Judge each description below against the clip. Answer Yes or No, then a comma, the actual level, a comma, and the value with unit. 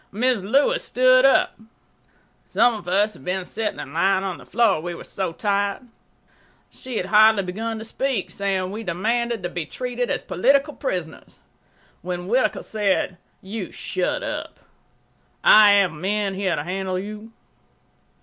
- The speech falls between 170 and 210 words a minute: No, average, 155 wpm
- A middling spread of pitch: Yes, average, 3.6 semitones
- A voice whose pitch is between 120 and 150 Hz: No, high, 200 Hz